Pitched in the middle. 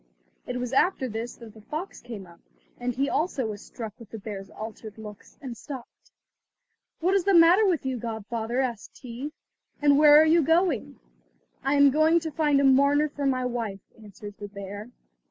No: very high, 250 Hz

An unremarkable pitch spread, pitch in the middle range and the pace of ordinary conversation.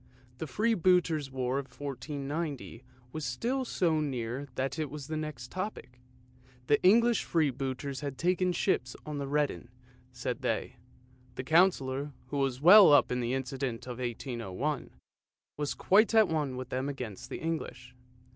Yes: average, 4.0 semitones; medium, 145 Hz; average, 150 wpm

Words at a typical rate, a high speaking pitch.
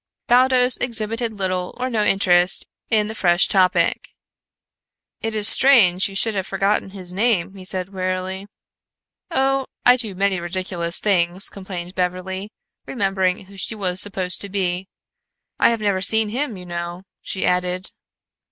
Yes: average, 150 wpm; high, 195 Hz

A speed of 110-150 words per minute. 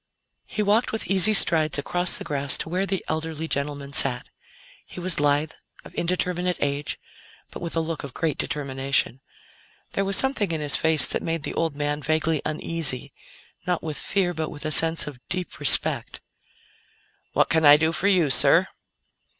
No: average, 175 wpm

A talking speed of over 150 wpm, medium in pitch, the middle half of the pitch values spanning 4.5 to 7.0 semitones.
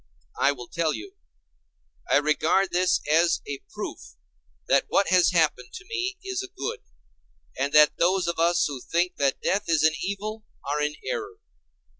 Yes: average, 170 wpm; medium, 170 Hz; wide, 5.6 semitones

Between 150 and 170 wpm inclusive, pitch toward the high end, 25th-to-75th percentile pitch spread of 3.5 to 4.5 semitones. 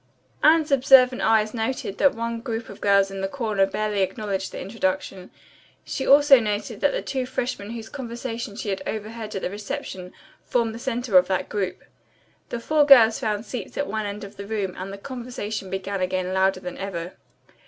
No: average, 190 wpm; high, 215 Hz; average, 3.8 semitones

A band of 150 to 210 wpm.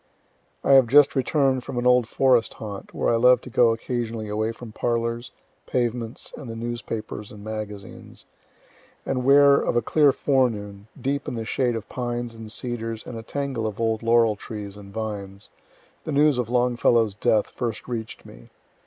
Yes: average, 175 wpm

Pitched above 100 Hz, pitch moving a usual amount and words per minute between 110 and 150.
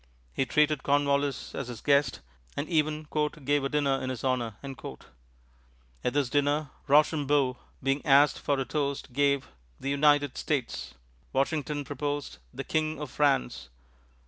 No: medium, 140 Hz; narrow, 1.6 semitones; average, 140 wpm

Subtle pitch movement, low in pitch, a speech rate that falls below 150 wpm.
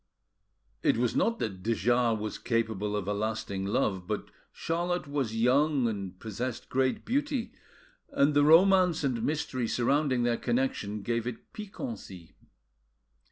No: average, 5.3 semitones; low, 120 Hz; average, 140 wpm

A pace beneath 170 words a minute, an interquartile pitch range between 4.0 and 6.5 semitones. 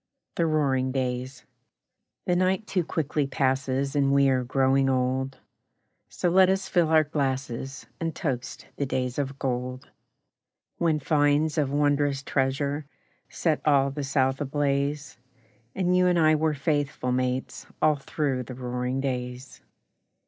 No: average, 140 wpm; narrow, 2.6 semitones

